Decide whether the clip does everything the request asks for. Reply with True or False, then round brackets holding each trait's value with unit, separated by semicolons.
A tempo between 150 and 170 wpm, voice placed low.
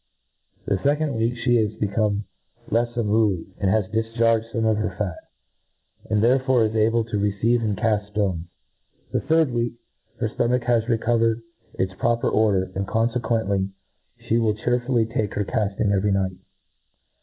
True (160 wpm; 110 Hz)